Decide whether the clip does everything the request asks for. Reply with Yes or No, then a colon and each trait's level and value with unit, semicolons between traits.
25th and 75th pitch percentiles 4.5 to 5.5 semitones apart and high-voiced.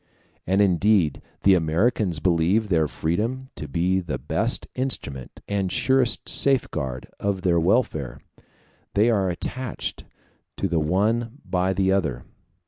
No: average, 4.8 semitones; very low, 95 Hz